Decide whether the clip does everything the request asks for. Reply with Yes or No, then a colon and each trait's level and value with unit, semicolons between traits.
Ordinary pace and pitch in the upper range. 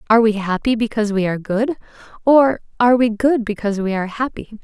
Yes: average, 195 wpm; high, 220 Hz